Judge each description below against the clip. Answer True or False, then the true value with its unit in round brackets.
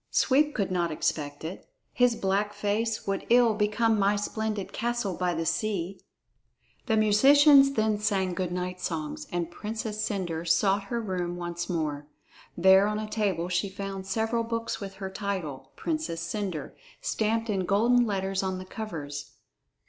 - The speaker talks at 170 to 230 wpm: False (155 wpm)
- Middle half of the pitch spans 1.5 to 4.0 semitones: True (3.5 semitones)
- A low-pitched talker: False (200 Hz)